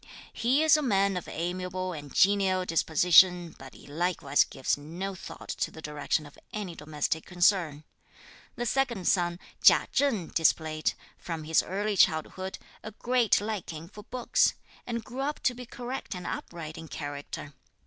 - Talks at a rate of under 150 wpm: No, average, 160 wpm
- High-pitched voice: No, medium, 180 Hz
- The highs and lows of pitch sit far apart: No, average, 5.0 semitones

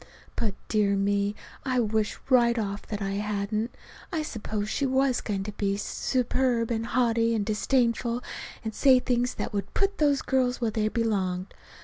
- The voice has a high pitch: Yes, high, 225 Hz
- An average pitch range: Yes, average, 3.4 semitones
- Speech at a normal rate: Yes, average, 165 wpm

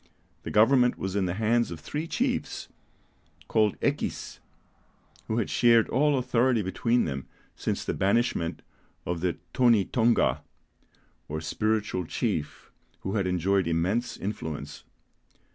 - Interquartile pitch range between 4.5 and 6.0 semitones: Yes, average, 4.8 semitones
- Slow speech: Yes, slow, 125 wpm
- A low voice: Yes, low, 105 Hz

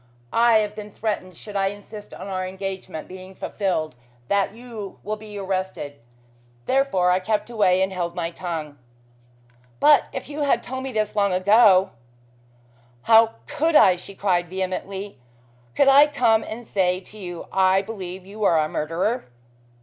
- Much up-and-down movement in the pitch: No, average, 3.0 semitones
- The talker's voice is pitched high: Yes, high, 195 Hz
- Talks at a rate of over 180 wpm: No, average, 165 wpm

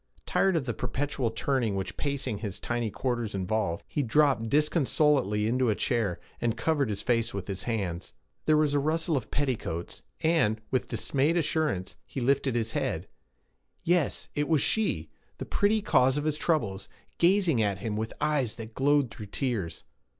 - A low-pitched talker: Yes, low, 130 Hz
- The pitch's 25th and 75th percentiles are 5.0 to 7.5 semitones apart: Yes, wide, 5.4 semitones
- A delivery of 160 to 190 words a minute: Yes, average, 170 wpm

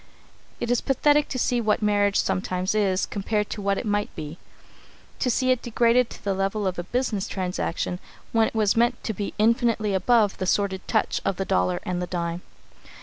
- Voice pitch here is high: Yes, high, 205 Hz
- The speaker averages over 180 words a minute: Yes, average, 200 wpm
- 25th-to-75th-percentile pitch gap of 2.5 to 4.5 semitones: Yes, average, 3.7 semitones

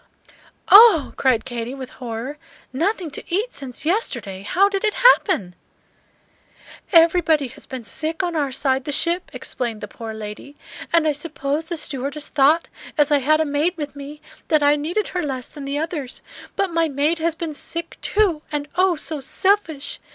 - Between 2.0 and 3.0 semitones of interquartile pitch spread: No, average, 3.9 semitones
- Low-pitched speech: No, very high, 300 Hz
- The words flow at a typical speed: Yes, average, 175 wpm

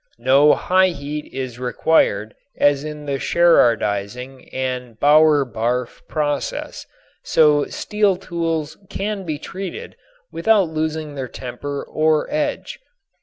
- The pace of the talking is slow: Yes, slow, 115 wpm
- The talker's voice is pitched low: No, medium, 150 Hz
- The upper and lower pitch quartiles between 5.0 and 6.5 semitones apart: No, average, 4.3 semitones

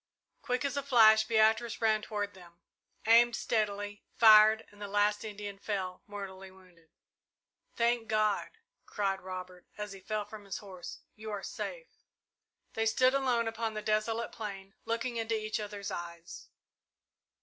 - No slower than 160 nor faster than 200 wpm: No, average, 150 wpm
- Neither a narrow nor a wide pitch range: No, narrow, 2.2 semitones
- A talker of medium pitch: No, high, 215 Hz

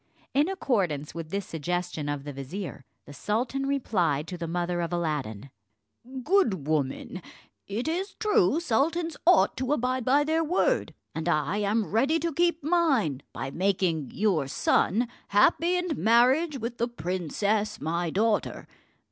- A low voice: No, high, 210 Hz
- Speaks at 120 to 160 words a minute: Yes, average, 150 wpm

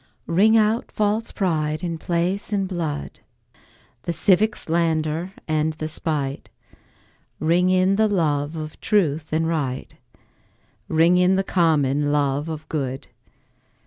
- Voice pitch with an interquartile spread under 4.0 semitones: Yes, average, 3.5 semitones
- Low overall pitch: No, medium, 165 Hz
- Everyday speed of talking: No, slow, 125 wpm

